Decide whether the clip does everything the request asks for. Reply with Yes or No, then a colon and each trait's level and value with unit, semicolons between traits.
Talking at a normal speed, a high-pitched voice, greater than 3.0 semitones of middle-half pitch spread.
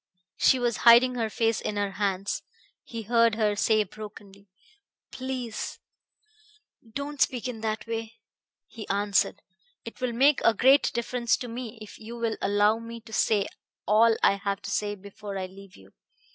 No: average, 165 wpm; high, 220 Hz; narrow, 2.5 semitones